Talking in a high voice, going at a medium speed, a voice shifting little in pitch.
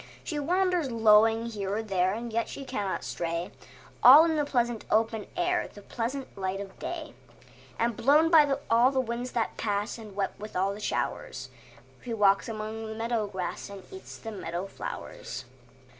No: high, 225 Hz; average, 175 wpm; average, 4.6 semitones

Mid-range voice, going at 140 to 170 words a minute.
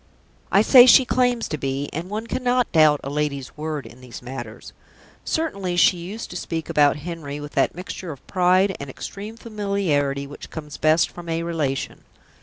No: medium, 165 Hz; average, 180 wpm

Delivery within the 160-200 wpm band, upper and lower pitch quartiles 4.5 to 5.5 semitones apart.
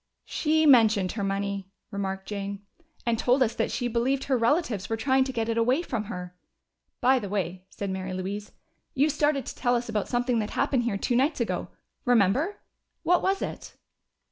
Yes: average, 190 wpm; average, 4.8 semitones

